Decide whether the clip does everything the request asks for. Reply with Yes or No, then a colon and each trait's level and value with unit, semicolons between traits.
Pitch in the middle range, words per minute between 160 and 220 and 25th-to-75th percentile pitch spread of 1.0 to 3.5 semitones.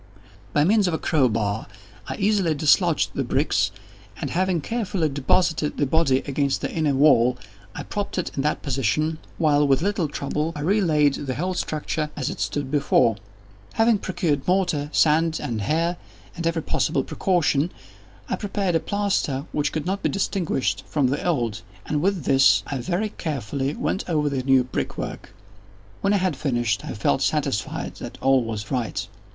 No: medium, 150 Hz; average, 175 wpm; average, 4.7 semitones